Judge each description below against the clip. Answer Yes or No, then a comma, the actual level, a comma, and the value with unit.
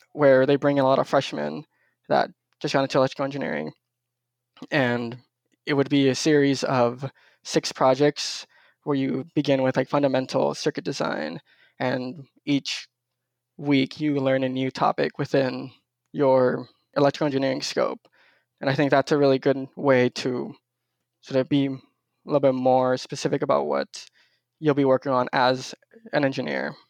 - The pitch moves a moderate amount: No, narrow, 1.8 semitones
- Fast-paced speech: No, average, 155 wpm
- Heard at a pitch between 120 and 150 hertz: Yes, low, 135 Hz